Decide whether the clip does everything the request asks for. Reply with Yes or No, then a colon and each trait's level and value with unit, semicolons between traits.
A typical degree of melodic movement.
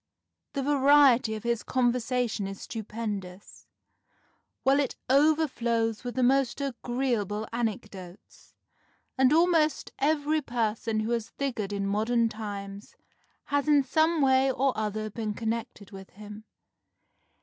Yes: average, 4.2 semitones